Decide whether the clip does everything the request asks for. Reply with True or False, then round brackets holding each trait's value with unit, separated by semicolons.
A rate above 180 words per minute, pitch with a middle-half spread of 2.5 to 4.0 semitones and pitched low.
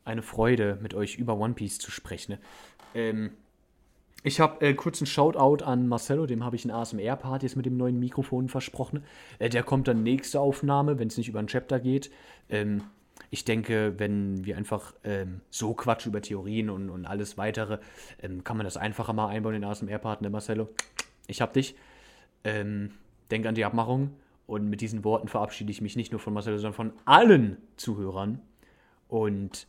True (190 wpm; 3.3 semitones; 110 Hz)